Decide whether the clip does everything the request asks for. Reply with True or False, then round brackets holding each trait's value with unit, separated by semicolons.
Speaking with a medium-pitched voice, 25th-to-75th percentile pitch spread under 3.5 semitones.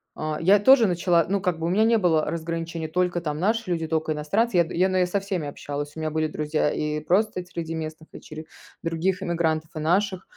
True (170 Hz; 2.9 semitones)